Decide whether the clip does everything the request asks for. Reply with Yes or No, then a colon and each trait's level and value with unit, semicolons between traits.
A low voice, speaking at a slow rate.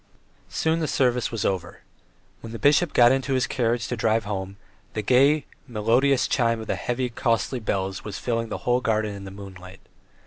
No: low, 115 Hz; average, 185 wpm